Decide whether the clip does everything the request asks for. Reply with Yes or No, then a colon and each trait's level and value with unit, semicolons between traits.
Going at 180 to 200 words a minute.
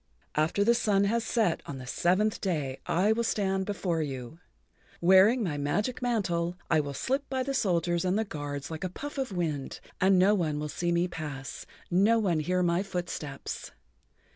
Yes: average, 185 wpm